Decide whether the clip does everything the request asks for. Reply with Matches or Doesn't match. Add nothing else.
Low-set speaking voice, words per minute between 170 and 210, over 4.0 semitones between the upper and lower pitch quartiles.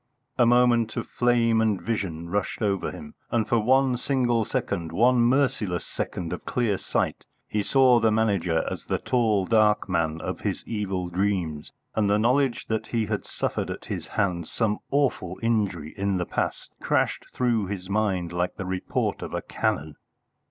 Matches